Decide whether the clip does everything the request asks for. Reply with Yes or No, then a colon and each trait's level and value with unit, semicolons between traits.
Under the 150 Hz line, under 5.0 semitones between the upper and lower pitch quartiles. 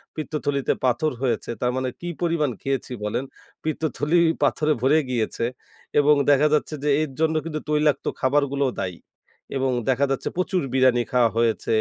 Yes: medium, 140 Hz; average, 3.2 semitones